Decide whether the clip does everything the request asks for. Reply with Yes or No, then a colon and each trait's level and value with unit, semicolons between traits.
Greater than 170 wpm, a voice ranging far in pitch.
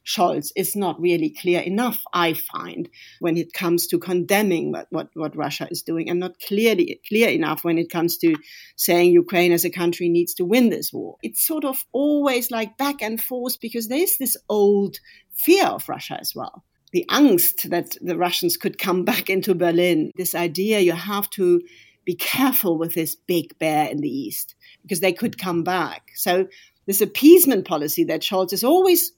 Yes: average, 190 wpm; wide, 5.7 semitones